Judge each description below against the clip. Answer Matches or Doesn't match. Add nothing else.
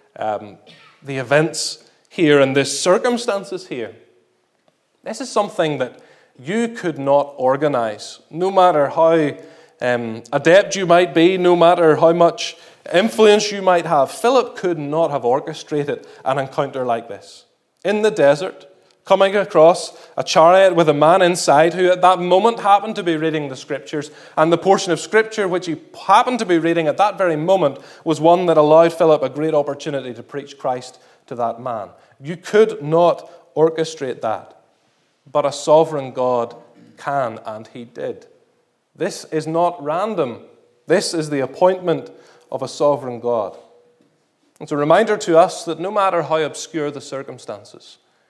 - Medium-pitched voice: Matches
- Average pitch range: Matches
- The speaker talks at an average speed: Matches